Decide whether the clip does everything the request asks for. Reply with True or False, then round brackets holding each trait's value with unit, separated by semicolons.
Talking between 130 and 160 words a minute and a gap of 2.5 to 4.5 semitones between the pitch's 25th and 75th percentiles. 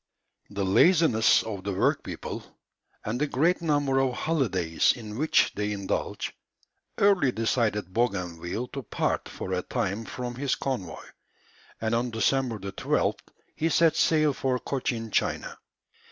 False (135 wpm; 5.1 semitones)